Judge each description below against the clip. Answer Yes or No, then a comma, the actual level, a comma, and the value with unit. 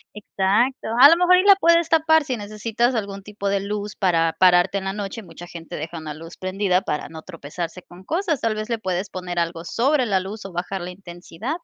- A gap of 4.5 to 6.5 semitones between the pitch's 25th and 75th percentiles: Yes, average, 4.8 semitones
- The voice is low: No, high, 195 Hz